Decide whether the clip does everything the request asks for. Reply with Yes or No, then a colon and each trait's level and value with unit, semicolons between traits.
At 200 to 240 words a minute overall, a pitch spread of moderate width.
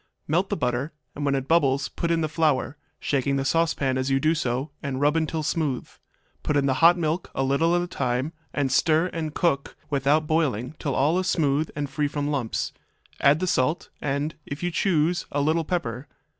Yes: fast, 205 wpm; average, 3.0 semitones